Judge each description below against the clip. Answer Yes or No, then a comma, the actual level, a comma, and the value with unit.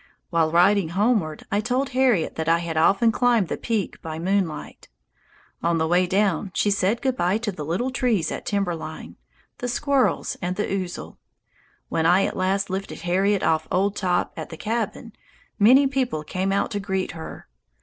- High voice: Yes, high, 195 Hz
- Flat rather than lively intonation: No, average, 4.6 semitones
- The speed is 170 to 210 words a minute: Yes, average, 180 wpm